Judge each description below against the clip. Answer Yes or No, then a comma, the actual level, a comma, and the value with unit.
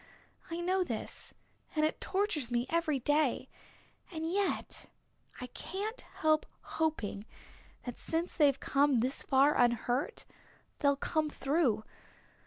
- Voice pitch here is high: Yes, very high, 295 Hz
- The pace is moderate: No, slow, 120 wpm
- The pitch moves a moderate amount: Yes, average, 4.9 semitones